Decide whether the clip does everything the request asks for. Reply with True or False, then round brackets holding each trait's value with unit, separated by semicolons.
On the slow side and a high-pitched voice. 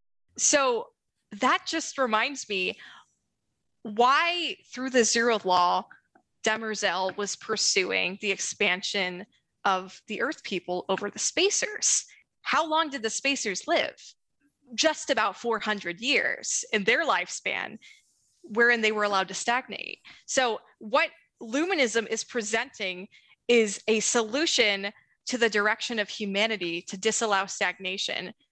True (120 wpm; 220 Hz)